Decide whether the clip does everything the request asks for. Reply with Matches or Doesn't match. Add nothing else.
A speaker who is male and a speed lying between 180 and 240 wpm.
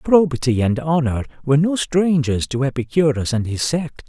Doesn't match